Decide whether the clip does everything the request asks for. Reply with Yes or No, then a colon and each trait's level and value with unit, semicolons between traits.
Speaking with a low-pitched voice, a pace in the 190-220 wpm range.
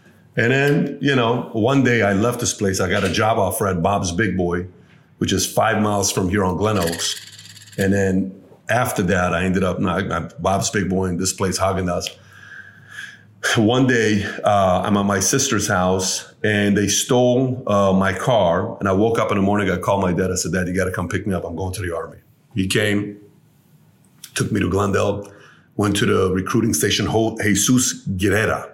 Yes: low, 100 Hz; average, 200 wpm